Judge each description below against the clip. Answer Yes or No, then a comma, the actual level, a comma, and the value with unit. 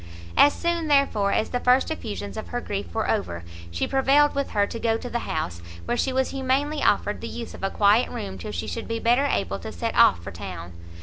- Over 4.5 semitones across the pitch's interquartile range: Yes, wide, 5.5 semitones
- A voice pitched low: No, high, 230 Hz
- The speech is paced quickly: Yes, fast, 235 wpm